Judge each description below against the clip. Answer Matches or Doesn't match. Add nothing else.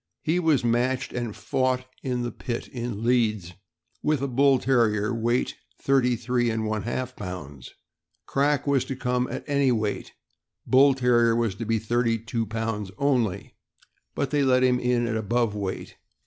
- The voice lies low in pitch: Matches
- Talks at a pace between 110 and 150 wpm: Doesn't match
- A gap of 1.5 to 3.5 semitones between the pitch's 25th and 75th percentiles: Matches